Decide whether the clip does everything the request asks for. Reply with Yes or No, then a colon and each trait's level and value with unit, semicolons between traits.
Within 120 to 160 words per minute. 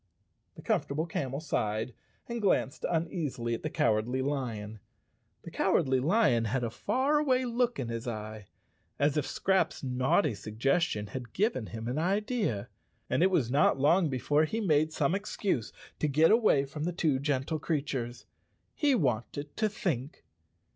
Yes: average, 155 wpm